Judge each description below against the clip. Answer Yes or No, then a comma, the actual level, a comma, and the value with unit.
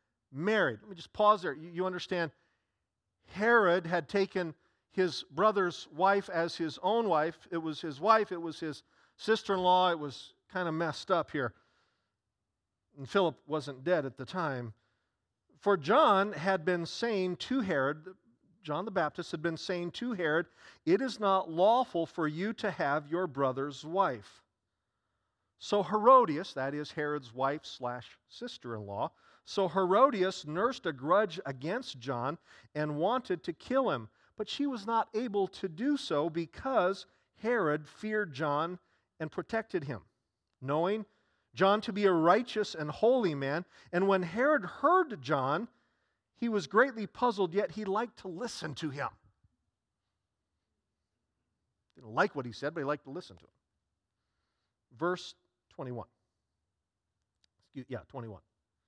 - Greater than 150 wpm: No, average, 145 wpm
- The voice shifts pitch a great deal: Yes, wide, 6.4 semitones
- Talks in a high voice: No, medium, 175 Hz